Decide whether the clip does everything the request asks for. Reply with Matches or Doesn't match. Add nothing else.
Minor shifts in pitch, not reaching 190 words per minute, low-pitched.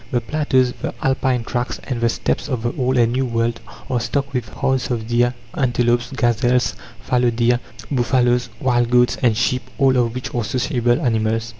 Matches